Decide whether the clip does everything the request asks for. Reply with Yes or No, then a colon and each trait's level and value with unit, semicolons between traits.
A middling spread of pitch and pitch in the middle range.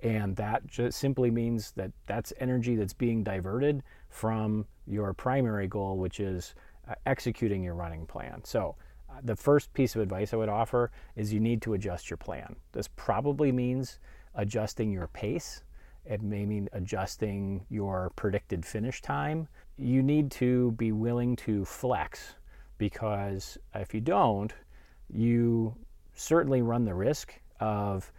No: average, 3.6 semitones; low, 110 Hz